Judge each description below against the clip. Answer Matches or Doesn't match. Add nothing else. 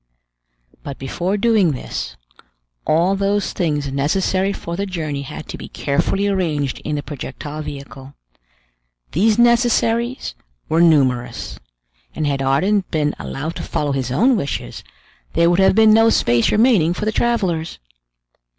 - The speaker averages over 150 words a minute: Doesn't match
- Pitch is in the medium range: Matches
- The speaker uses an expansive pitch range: Matches